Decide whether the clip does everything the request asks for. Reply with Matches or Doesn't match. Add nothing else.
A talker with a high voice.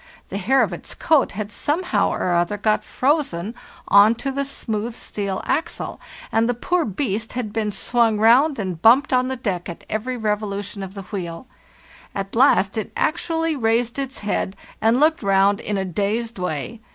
Matches